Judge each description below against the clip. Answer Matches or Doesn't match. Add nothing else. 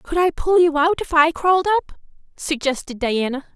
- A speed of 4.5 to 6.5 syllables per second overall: Matches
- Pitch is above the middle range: Matches